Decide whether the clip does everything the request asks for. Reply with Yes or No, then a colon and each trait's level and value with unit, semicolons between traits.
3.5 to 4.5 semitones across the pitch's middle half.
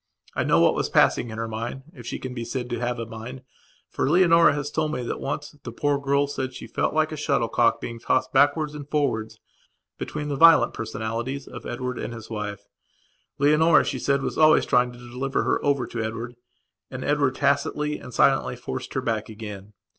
Yes: average, 3.9 semitones